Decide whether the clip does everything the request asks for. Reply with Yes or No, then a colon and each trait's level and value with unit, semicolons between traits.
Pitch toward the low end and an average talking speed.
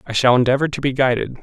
No: low, 130 Hz; fast, 255 wpm